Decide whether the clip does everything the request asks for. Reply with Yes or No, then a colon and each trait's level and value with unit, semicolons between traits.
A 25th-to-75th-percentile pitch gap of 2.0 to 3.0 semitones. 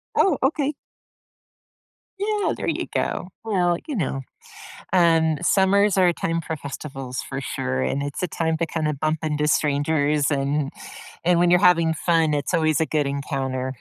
No: average, 3.7 semitones